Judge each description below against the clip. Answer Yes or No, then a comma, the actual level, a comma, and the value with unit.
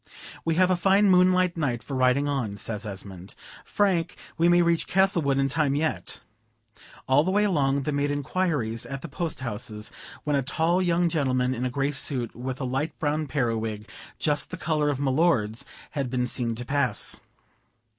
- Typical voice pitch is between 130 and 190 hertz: Yes, medium, 140 Hz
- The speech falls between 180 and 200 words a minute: Yes, average, 185 wpm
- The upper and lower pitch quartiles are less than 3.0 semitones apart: No, average, 5.0 semitones